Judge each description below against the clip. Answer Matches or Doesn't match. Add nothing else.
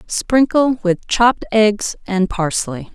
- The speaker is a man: Doesn't match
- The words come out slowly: Matches